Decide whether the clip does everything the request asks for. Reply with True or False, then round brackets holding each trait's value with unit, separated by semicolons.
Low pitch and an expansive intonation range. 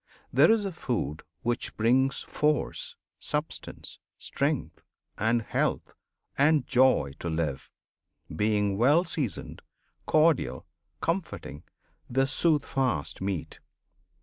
True (130 Hz; 6.9 semitones)